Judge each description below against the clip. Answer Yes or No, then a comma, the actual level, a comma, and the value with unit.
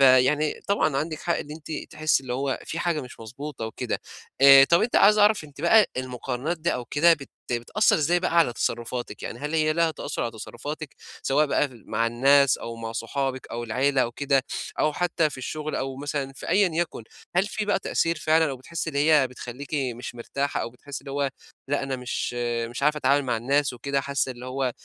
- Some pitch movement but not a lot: Yes, average, 3.5 semitones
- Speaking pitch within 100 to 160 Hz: Yes, medium, 140 Hz